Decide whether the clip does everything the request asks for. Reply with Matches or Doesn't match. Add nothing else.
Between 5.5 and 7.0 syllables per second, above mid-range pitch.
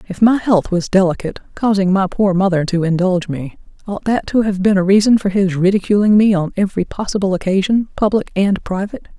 Matches